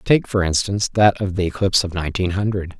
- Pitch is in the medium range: No, very low, 95 Hz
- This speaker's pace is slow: No, fast, 215 wpm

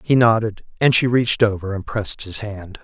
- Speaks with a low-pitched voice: Yes, low, 110 Hz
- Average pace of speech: No, fast, 210 wpm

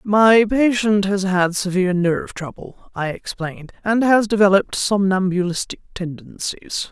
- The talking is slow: Yes, slow, 120 wpm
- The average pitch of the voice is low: No, high, 195 Hz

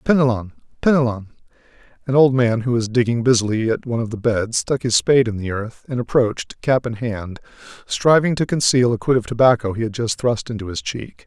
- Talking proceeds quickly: Yes, fast, 210 wpm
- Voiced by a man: Yes, male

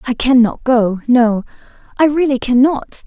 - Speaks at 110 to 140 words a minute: Yes, slow, 135 wpm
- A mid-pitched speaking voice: No, very high, 250 Hz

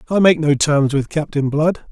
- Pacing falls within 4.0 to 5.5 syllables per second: Yes, 4.8 syllables/s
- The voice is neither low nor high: Yes, medium, 150 Hz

